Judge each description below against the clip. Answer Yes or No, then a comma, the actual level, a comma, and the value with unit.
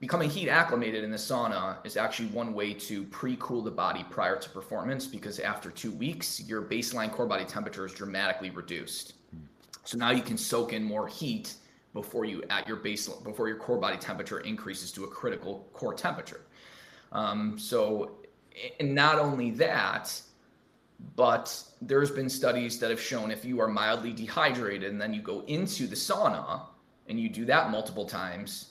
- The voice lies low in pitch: Yes, low, 120 Hz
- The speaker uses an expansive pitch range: Yes, wide, 5.9 semitones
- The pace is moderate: Yes, average, 175 wpm